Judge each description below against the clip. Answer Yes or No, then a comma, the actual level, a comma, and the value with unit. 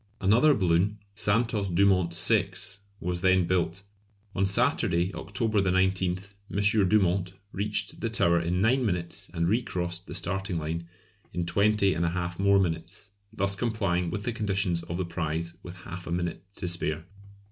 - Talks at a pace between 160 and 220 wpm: No, average, 150 wpm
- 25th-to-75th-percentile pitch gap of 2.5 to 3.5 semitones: Yes, average, 2.8 semitones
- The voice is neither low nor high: No, very low, 95 Hz